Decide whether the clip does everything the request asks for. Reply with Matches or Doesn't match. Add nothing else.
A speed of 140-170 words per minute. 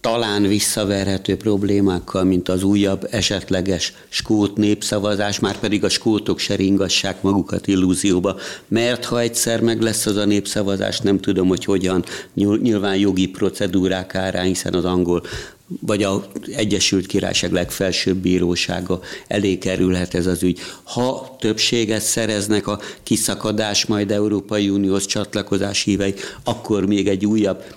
Doesn't match